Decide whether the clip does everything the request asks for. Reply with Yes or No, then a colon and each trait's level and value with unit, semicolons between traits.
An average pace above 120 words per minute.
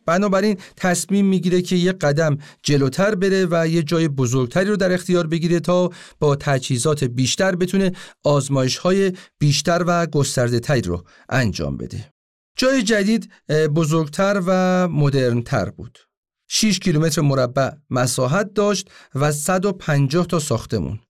Yes: average, 130 wpm